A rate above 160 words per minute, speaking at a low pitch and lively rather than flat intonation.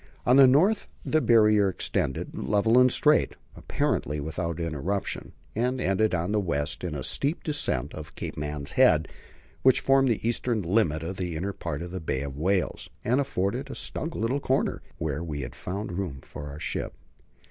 Yes: average, 180 wpm; very low, 95 Hz; wide, 7.8 semitones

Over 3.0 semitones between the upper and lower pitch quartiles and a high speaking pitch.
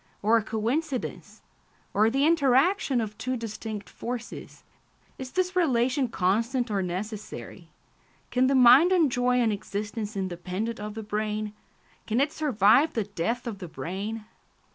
Yes: average, 3.8 semitones; high, 230 Hz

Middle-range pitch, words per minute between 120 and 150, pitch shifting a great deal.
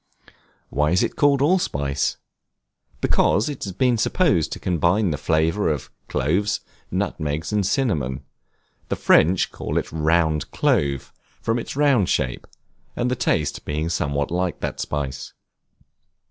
No: very low, 85 Hz; slow, 135 wpm; wide, 6.6 semitones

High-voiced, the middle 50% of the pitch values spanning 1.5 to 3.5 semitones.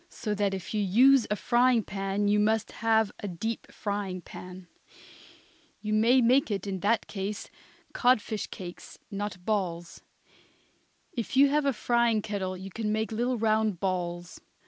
Yes: high, 210 Hz; average, 2.9 semitones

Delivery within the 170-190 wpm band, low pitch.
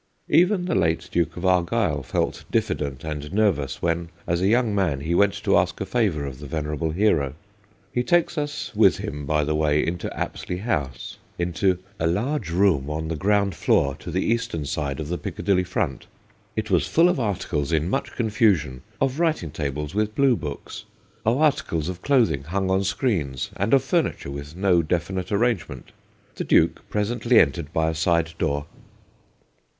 Yes: average, 180 wpm; very low, 85 Hz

